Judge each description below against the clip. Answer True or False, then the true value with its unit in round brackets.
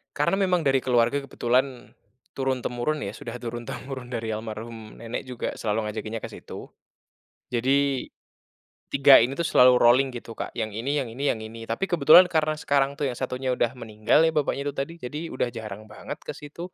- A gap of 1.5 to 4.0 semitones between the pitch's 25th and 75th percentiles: True (3.5 semitones)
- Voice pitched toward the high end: False (125 Hz)